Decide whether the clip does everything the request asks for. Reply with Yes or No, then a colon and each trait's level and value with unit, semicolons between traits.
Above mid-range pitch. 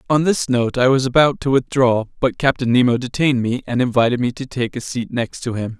No: low, 125 Hz